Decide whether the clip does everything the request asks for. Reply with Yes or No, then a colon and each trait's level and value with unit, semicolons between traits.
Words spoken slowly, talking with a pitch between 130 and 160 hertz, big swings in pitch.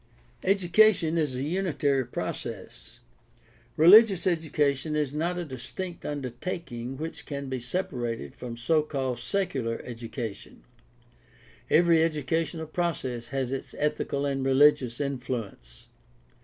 No: slow, 115 wpm; medium, 140 Hz; average, 4.7 semitones